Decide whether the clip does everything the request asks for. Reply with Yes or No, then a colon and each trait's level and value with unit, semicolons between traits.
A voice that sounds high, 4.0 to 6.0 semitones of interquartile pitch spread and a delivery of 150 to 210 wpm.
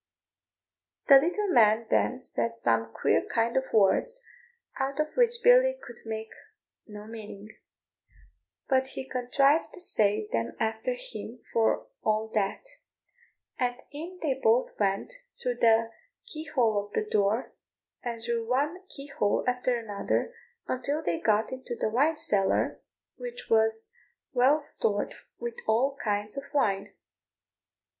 No: high, 240 Hz; average, 5.1 semitones; slow, 135 wpm